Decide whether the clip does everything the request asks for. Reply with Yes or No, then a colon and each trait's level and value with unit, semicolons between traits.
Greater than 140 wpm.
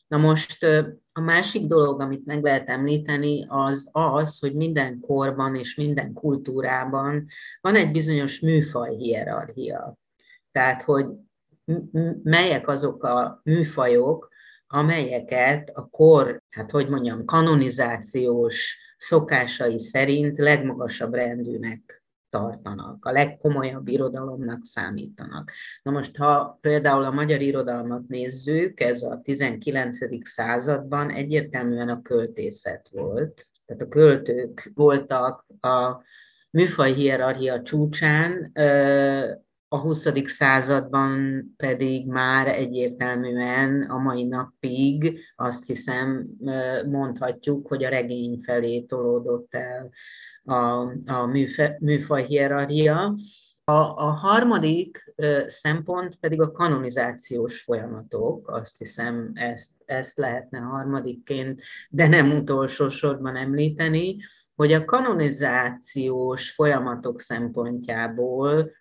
No: slow, 105 wpm